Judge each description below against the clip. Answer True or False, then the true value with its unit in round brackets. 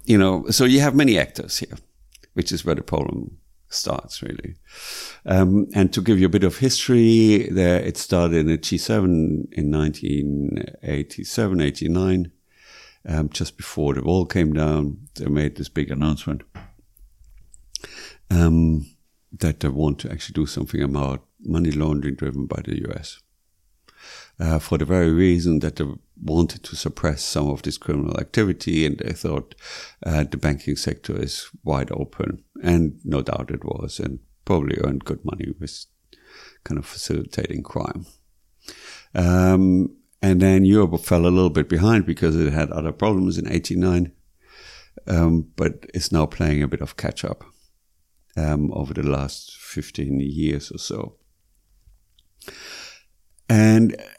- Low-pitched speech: True (80 Hz)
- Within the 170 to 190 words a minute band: False (150 wpm)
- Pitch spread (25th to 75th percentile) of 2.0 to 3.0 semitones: False (3.6 semitones)